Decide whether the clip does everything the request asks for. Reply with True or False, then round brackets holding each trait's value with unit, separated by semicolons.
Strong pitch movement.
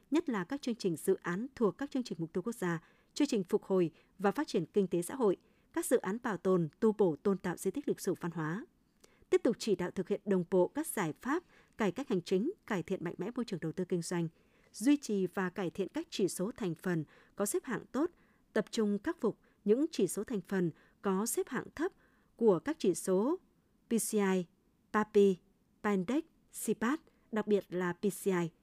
False (4.1 semitones)